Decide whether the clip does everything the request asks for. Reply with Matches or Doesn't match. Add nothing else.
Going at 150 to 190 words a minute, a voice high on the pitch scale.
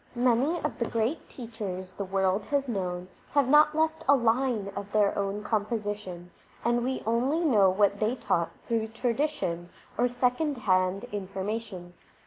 Matches